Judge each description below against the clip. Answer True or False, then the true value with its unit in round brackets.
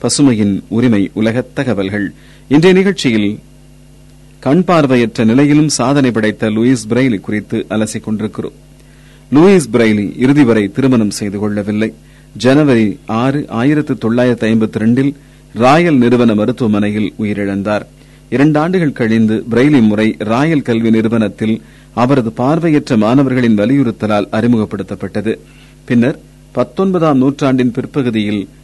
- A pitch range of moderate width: True (4.1 semitones)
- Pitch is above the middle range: False (115 Hz)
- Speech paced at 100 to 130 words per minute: False (90 wpm)